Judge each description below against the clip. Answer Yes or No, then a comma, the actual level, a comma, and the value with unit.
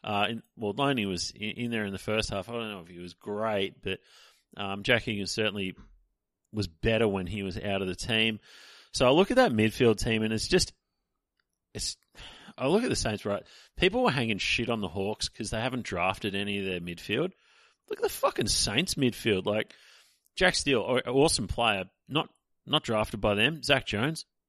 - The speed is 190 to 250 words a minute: Yes, fast, 205 wpm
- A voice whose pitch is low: Yes, low, 110 Hz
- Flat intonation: No, average, 3.2 semitones